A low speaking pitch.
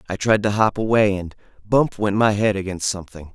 Yes: low, 100 Hz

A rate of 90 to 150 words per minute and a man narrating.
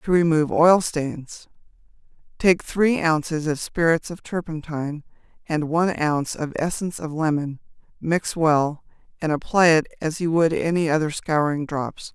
No: average, 145 wpm; female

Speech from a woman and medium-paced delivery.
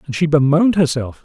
No: male; average, 195 wpm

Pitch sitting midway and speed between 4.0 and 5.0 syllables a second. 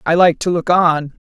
Yes: medium, 165 Hz; 4.7 syllables/s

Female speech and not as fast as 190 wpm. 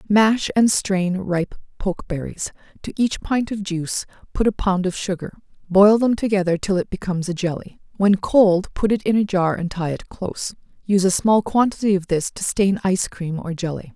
No: female; average, 200 wpm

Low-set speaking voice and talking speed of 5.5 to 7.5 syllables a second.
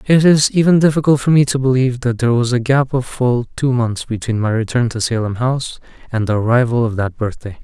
Yes: low, 125 Hz; 5.9 syllables/s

